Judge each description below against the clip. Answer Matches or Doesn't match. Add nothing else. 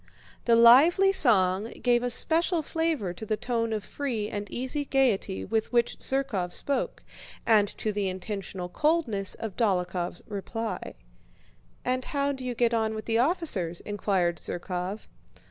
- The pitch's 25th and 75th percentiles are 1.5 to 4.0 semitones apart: Doesn't match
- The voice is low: Doesn't match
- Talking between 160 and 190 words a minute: Doesn't match